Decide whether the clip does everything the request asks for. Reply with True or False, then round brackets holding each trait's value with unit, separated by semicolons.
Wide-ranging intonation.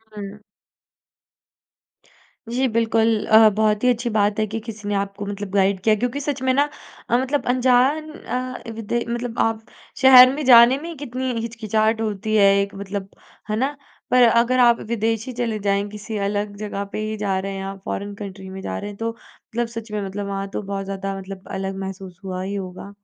False (3.2 semitones)